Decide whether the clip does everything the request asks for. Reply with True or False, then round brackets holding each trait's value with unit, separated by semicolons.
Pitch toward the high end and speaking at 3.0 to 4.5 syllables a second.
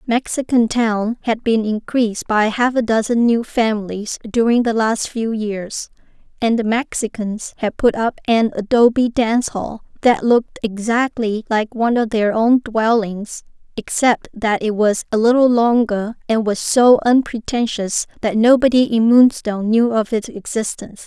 True (225 Hz; 4.4 syllables/s)